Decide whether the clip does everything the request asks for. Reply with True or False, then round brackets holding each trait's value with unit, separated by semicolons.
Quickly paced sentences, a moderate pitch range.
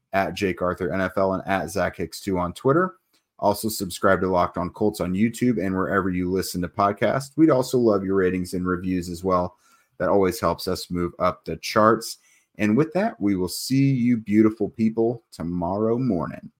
False (175 wpm; 3.3 semitones)